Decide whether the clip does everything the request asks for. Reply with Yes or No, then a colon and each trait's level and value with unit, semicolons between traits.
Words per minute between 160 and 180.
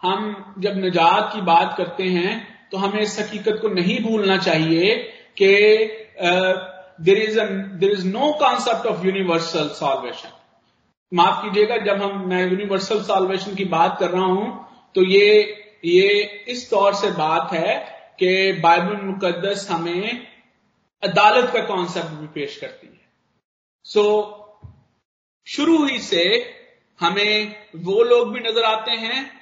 No: average, 140 wpm